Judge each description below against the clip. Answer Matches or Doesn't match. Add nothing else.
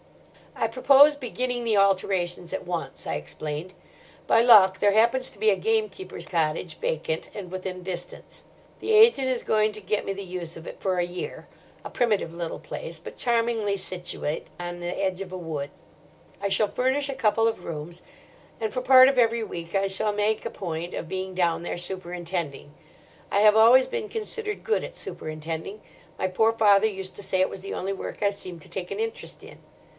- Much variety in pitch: Doesn't match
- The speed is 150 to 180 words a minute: Doesn't match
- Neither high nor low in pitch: Doesn't match